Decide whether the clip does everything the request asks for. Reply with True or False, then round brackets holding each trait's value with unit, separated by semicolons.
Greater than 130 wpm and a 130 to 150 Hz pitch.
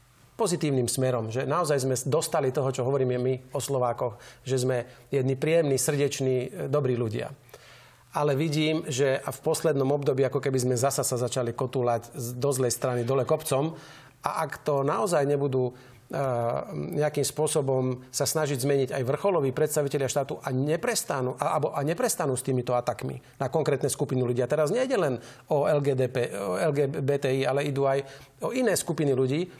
True (160 wpm; 135 Hz)